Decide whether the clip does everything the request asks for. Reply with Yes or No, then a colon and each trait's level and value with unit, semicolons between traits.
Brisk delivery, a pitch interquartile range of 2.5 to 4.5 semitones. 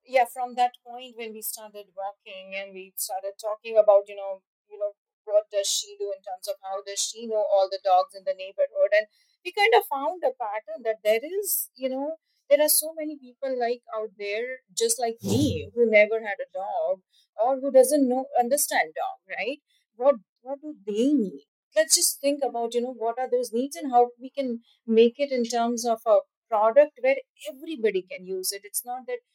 No: fast, 210 wpm; wide, 5.5 semitones